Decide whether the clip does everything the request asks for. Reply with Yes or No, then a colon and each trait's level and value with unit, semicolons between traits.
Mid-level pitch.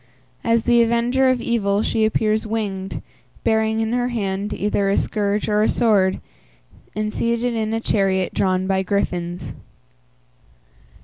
No: high, 215 Hz